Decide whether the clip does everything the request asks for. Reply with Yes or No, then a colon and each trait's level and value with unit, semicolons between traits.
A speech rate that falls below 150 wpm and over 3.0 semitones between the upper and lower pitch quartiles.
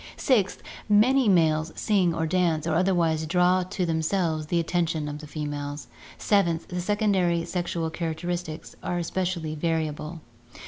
No: slow, 135 wpm; narrow, 2.5 semitones